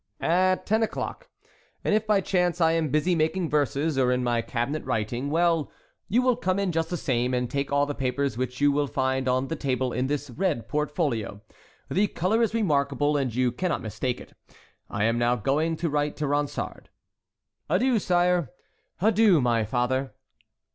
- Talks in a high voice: No, medium, 145 Hz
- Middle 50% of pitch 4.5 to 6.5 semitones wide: Yes, wide, 5.6 semitones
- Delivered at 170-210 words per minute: Yes, average, 180 wpm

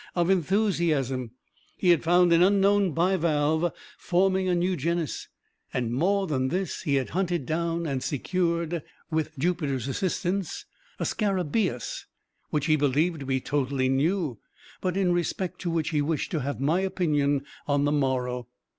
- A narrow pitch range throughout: No, average, 4.2 semitones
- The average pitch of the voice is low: No, medium, 165 Hz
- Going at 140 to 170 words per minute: Yes, average, 155 wpm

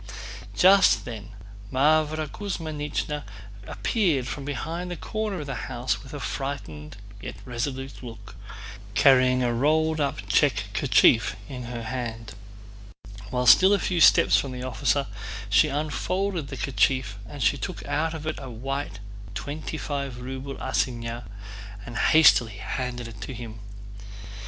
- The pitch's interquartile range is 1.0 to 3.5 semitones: No, average, 4.2 semitones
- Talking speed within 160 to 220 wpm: No, slow, 135 wpm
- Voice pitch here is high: No, low, 135 Hz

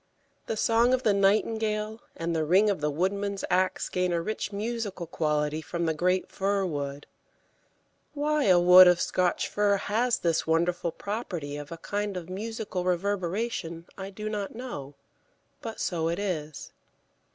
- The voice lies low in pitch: No, medium, 185 Hz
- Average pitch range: Yes, average, 4.0 semitones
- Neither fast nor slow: Yes, average, 160 wpm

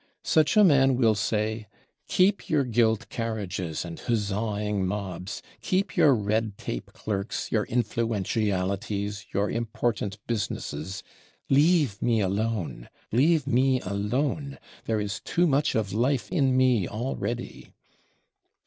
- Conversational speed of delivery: No, slow, 120 wpm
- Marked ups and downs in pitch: No, average, 4.3 semitones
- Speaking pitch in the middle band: No, low, 110 Hz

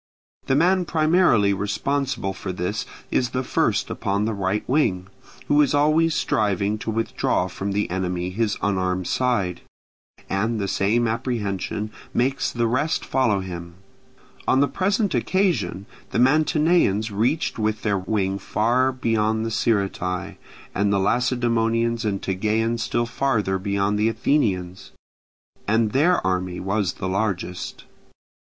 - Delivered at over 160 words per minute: No, slow, 135 wpm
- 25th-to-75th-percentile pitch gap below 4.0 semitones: No, average, 4.6 semitones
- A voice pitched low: Yes, low, 110 Hz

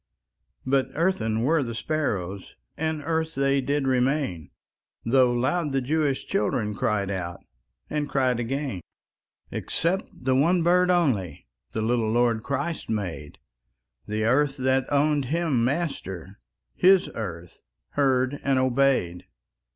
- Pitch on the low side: Yes, low, 130 Hz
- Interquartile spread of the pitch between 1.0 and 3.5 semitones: No, average, 5.2 semitones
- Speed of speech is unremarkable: No, slow, 125 wpm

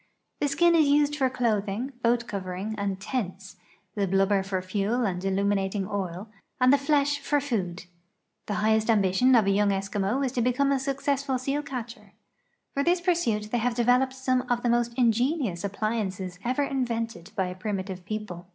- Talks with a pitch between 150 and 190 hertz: No, high, 225 Hz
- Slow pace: No, average, 175 wpm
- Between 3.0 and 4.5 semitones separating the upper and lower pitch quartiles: No, average, 5.0 semitones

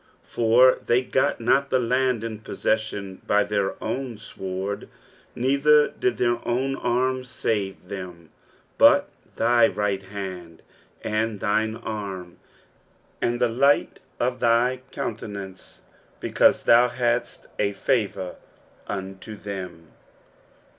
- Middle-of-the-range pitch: No, low, 110 Hz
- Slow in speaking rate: Yes, slow, 115 wpm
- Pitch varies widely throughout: No, average, 3.9 semitones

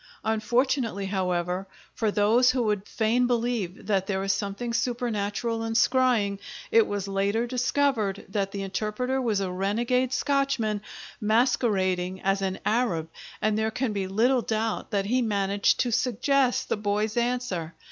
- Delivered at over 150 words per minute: No, average, 145 wpm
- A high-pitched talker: Yes, high, 215 Hz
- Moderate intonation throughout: Yes, average, 3.6 semitones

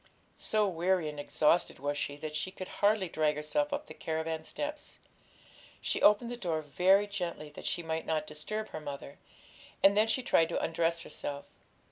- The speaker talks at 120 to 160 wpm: No, average, 180 wpm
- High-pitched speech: No, medium, 165 Hz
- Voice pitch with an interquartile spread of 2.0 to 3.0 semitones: No, average, 5.0 semitones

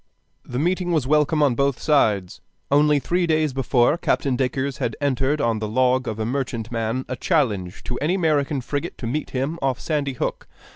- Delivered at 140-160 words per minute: No, average, 185 wpm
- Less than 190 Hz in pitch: Yes, low, 135 Hz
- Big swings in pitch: No, average, 3.6 semitones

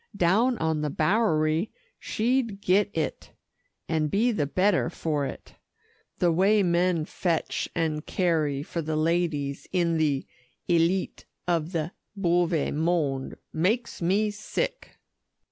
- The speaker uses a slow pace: Yes, slow, 125 wpm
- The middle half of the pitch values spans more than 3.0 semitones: Yes, average, 4.0 semitones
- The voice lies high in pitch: No, medium, 170 Hz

